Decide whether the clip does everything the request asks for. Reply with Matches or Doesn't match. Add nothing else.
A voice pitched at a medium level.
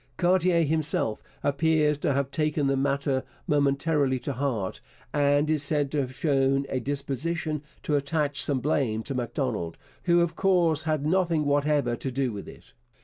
Matches